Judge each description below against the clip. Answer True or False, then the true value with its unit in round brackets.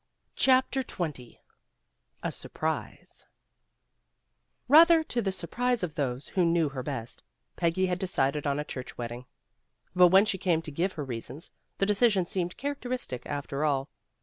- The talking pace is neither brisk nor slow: True (150 wpm)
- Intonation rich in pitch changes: True (6.5 semitones)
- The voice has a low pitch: False (170 Hz)